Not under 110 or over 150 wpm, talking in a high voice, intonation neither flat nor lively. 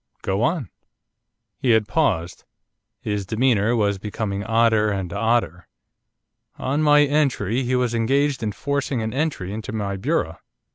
No: average, 140 wpm; low, 115 Hz; average, 4.7 semitones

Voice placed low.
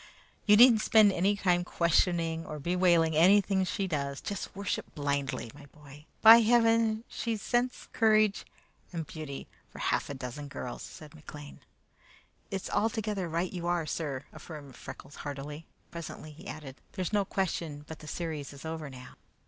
No: medium, 170 Hz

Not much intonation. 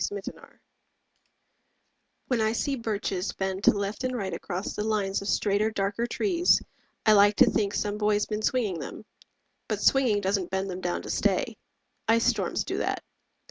Yes: narrow, 2.2 semitones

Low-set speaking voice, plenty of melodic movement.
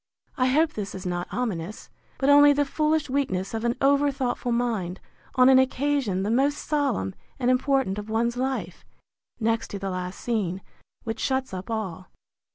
No: high, 240 Hz; wide, 5.8 semitones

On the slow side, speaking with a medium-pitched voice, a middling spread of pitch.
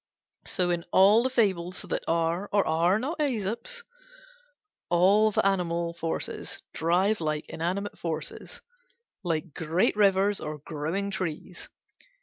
Yes: slow, 125 wpm; medium, 180 Hz; average, 3.5 semitones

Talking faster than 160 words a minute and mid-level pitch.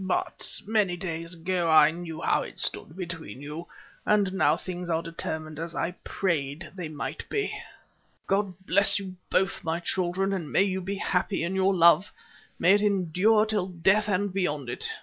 Yes: average, 170 wpm; medium, 180 Hz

